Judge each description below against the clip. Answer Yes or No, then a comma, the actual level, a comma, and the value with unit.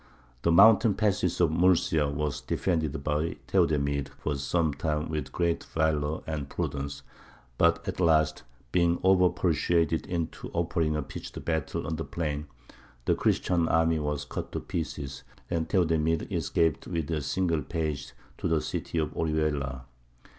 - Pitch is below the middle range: Yes, very low, 80 Hz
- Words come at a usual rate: Yes, average, 145 wpm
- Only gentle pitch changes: Yes, narrow, 2.2 semitones